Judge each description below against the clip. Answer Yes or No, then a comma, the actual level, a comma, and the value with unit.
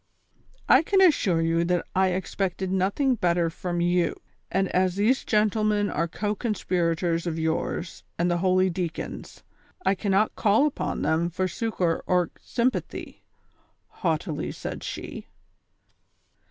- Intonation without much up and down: No, average, 3.3 semitones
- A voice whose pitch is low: No, medium, 185 Hz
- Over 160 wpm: No, slow, 135 wpm